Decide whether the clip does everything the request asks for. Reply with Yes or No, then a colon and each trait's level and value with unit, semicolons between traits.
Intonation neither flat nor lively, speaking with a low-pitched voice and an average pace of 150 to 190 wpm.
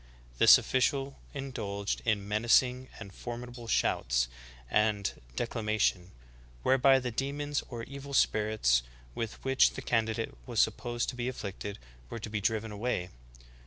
No: average, 3.7 semitones; low, 115 Hz; slow, 135 wpm